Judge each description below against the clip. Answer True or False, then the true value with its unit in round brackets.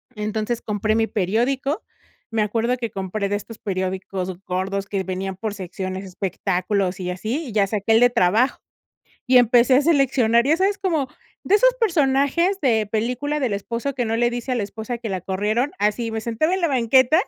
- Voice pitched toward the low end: False (225 Hz)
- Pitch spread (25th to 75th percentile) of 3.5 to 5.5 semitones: True (4.7 semitones)